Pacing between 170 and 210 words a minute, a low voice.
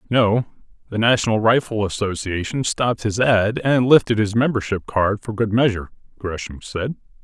No: average, 150 wpm; low, 110 Hz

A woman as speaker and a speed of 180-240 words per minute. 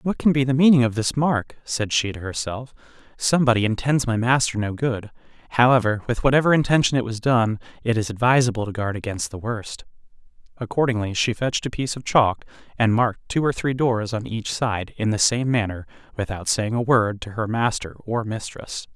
No: male; average, 195 wpm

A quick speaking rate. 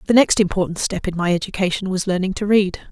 Yes: fast, 225 wpm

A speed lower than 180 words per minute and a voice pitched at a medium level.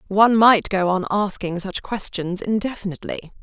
No: average, 140 wpm; high, 195 Hz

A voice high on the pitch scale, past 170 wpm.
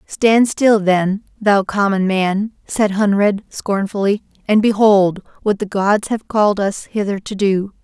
No: high, 205 Hz; average, 155 wpm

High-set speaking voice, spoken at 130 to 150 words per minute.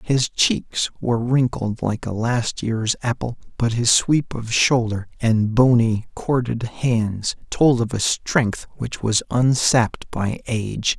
No: low, 115 Hz; average, 145 wpm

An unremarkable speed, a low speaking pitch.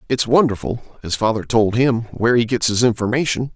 Yes: average, 170 wpm; low, 115 Hz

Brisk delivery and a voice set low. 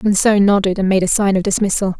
No: fast, 240 wpm; high, 195 Hz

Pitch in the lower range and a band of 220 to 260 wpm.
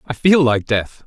Yes: low, 130 Hz; fast, 225 wpm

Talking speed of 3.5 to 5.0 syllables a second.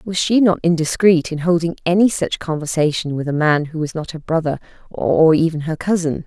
No: 5.4 syllables/s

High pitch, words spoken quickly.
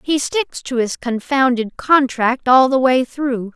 No: very high, 255 Hz; average, 170 wpm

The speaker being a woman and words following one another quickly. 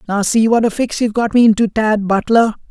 No: male; fast, 245 wpm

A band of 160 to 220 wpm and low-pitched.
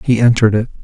Yes: fast, 215 wpm; low, 115 Hz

